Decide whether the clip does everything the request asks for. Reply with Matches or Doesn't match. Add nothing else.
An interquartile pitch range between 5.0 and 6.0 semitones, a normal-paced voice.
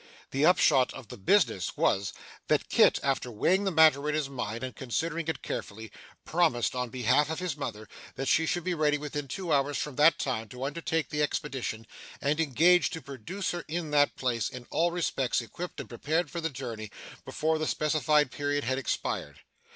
Doesn't match